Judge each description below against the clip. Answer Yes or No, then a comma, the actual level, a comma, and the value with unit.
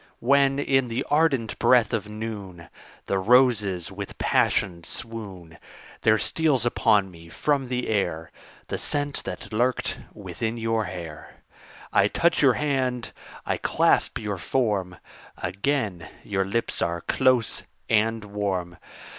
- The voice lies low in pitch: Yes, low, 110 Hz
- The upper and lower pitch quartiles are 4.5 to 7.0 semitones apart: Yes, average, 4.8 semitones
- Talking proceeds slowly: Yes, slow, 130 wpm